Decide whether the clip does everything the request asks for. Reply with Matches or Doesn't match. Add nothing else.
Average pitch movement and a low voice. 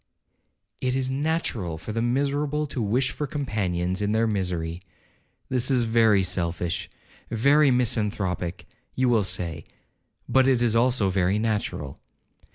Doesn't match